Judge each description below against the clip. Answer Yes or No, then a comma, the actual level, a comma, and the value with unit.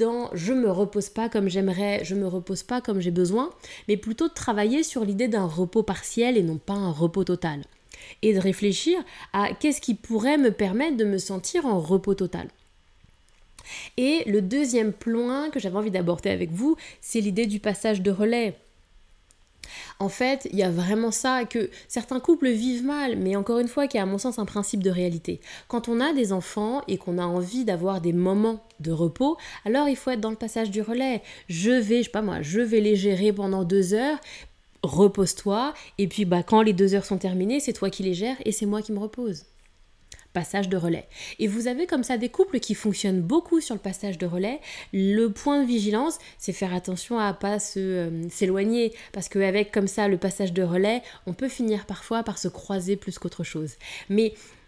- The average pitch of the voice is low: No, high, 210 Hz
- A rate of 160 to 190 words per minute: No, average, 210 wpm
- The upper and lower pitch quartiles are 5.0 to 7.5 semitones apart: No, average, 3.7 semitones